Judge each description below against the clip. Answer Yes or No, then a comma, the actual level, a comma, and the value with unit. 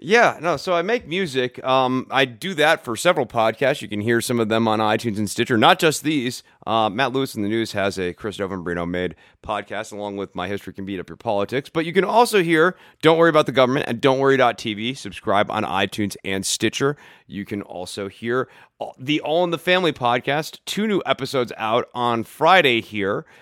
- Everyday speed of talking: No, fast, 210 wpm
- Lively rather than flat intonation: Yes, wide, 6.6 semitones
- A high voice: No, low, 120 Hz